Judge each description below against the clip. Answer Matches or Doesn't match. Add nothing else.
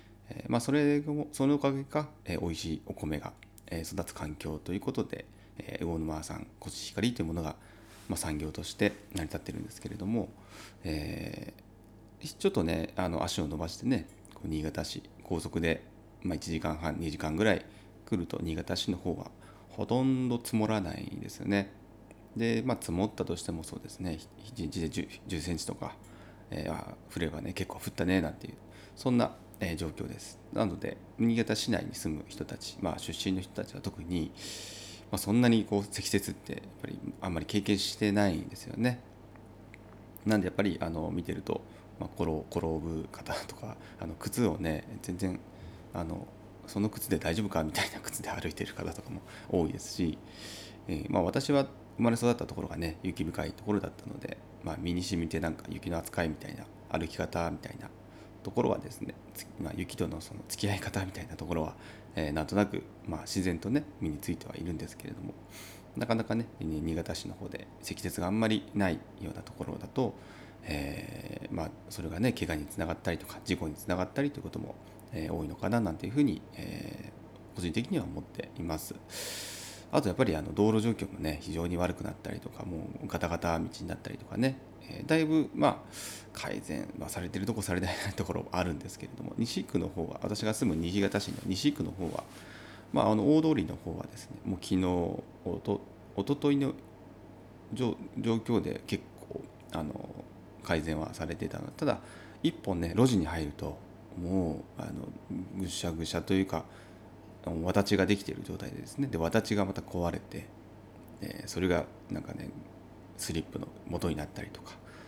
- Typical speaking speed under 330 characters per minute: Doesn't match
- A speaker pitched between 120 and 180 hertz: Doesn't match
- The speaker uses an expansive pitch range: Doesn't match